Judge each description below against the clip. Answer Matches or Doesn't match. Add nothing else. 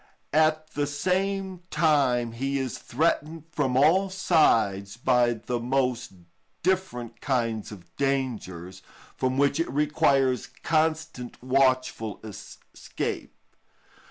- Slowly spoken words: Matches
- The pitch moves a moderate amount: Matches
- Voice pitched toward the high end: Doesn't match